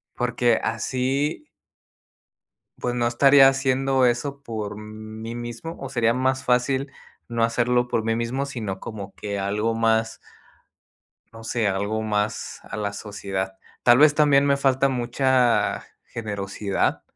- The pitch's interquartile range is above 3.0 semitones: Yes, average, 3.4 semitones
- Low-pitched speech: Yes, low, 120 Hz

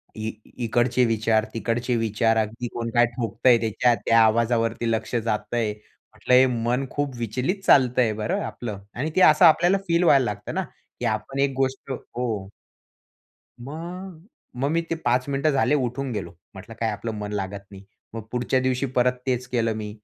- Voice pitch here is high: No, low, 120 Hz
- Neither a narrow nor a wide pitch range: Yes, average, 3.0 semitones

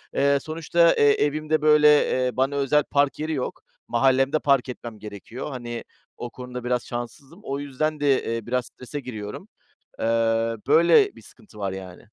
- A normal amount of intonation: Yes, average, 3.6 semitones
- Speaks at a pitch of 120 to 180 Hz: Yes, low, 135 Hz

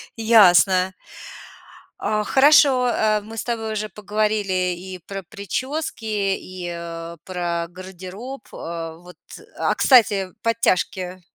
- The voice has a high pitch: Yes, high, 195 Hz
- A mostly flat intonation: No, average, 3.6 semitones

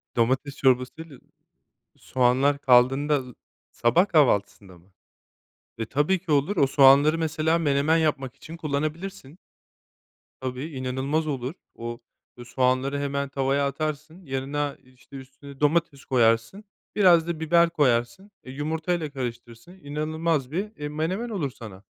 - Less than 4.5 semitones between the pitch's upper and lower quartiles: Yes, average, 3.7 semitones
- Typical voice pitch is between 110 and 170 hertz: Yes, medium, 140 Hz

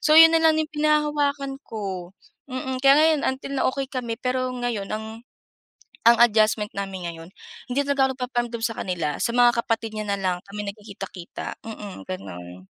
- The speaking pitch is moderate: No, high, 235 Hz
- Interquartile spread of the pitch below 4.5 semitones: No, average, 5.3 semitones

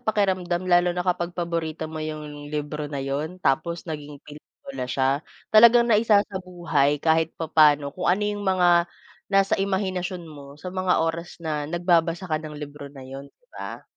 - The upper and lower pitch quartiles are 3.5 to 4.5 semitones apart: Yes, average, 3.8 semitones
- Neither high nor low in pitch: Yes, medium, 165 Hz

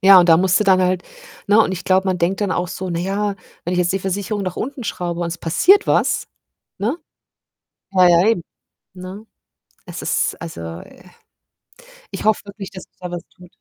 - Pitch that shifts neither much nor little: No, narrow, 2.2 semitones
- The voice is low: No, medium, 185 Hz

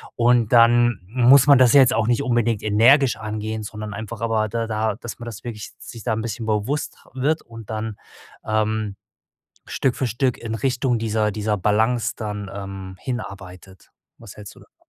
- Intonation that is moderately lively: No, narrow, 2.1 semitones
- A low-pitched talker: Yes, low, 110 Hz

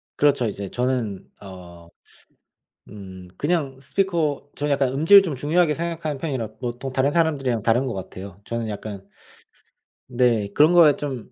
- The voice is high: No, low, 130 Hz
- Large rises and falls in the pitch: Yes, wide, 5.7 semitones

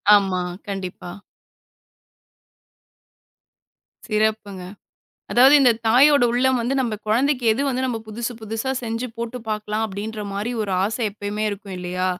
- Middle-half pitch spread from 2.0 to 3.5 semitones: Yes, average, 3.2 semitones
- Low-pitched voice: No, high, 220 Hz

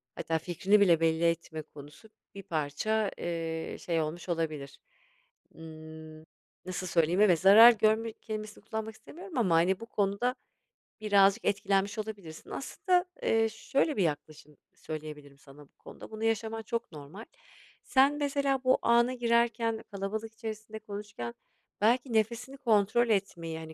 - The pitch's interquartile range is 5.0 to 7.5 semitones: Yes, wide, 5.6 semitones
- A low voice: No, high, 205 Hz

